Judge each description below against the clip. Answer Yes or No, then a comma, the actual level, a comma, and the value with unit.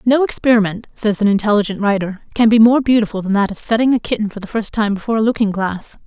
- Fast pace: Yes, fast, 235 wpm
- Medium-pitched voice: No, high, 215 Hz